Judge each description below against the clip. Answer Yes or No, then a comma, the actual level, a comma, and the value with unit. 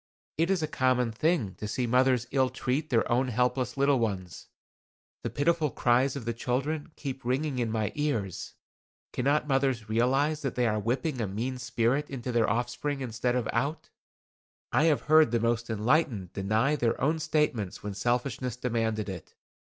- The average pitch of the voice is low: Yes, low, 125 Hz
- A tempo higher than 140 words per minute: Yes, average, 170 wpm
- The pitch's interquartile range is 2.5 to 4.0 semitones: Yes, average, 3.6 semitones